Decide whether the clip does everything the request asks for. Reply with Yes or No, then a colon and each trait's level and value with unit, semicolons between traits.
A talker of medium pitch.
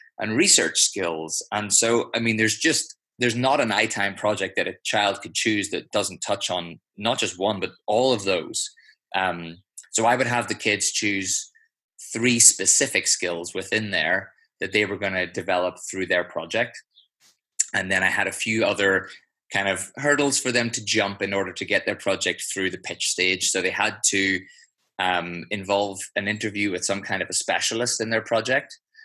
No: low, 100 Hz